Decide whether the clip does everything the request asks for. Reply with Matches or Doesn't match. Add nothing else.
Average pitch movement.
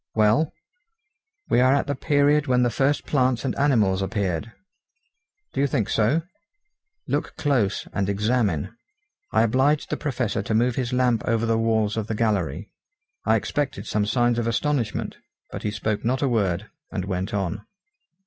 Matches